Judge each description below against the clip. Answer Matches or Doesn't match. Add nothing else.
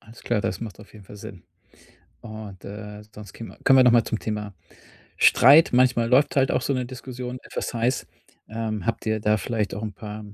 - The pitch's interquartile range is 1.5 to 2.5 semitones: Doesn't match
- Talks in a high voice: Doesn't match